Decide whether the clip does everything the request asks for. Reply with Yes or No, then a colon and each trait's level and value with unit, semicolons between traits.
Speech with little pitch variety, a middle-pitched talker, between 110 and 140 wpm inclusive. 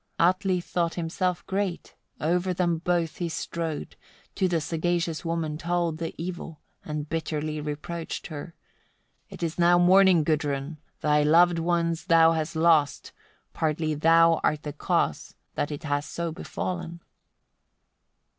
Yes: narrow, 2.0 semitones; medium, 165 Hz; slow, 135 wpm